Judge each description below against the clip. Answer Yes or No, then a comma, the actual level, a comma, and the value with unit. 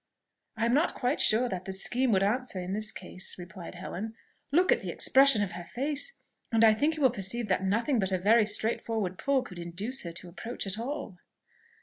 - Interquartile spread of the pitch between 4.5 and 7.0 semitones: Yes, average, 5.0 semitones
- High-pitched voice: Yes, high, 220 Hz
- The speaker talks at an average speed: No, fast, 215 wpm